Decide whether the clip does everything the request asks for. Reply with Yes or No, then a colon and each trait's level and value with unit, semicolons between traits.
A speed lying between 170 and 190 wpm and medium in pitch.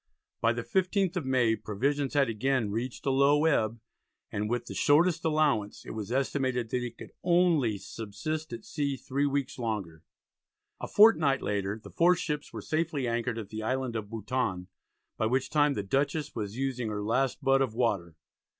No: average, 180 wpm; low, 130 Hz